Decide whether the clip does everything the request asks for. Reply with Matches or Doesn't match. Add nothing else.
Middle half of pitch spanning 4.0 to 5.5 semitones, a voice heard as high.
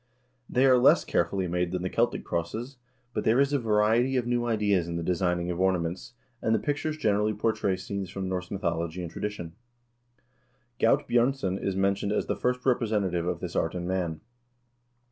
Doesn't match